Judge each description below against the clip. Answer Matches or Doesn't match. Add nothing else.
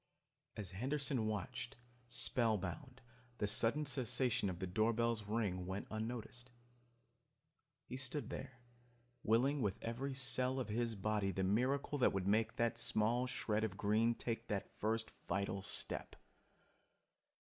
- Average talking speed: Doesn't match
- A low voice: Matches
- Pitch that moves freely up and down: Doesn't match